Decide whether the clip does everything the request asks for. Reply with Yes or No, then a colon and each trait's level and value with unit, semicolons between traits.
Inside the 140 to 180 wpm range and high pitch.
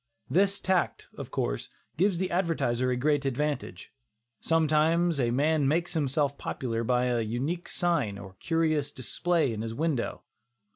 No: average, 150 wpm; medium, 145 Hz